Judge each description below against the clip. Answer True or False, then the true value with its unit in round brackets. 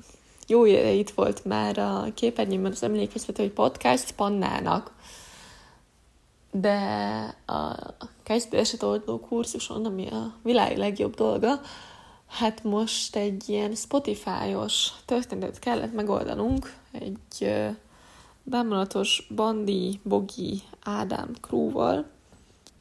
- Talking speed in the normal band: False (95 wpm)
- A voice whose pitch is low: False (210 Hz)